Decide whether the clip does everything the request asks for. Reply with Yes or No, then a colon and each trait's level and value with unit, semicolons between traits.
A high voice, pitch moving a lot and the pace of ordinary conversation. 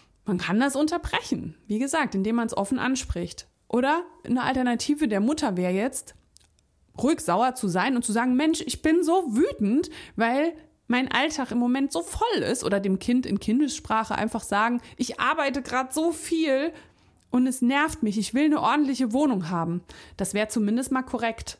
Yes: very high, 250 Hz; wide, 5.8 semitones; average, 180 wpm